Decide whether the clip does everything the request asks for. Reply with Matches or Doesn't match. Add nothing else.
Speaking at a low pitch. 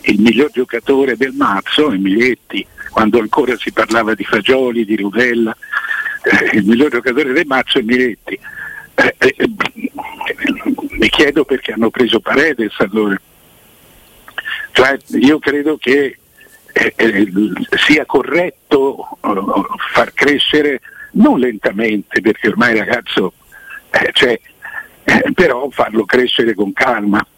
Matches